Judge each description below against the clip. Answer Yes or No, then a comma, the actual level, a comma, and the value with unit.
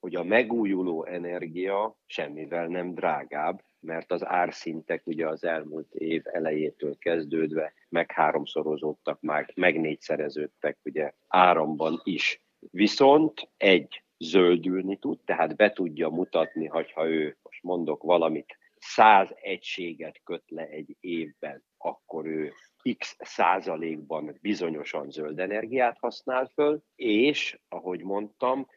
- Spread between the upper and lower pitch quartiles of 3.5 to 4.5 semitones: Yes, average, 3.9 semitones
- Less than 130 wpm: Yes, average, 115 wpm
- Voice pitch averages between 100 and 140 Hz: No, very low, 85 Hz